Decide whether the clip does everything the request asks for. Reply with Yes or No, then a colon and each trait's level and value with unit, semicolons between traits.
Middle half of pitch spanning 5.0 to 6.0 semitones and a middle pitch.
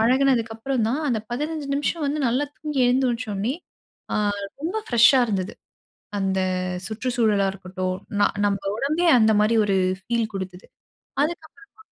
No: average, 5.3 semitones; high, 235 Hz